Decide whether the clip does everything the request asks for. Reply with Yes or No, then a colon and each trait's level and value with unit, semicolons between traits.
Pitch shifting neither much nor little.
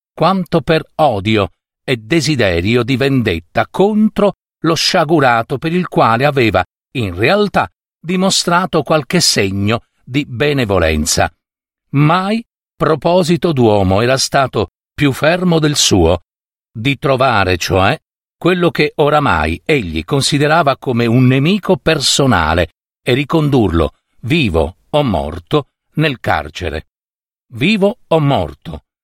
No: wide, 7.0 semitones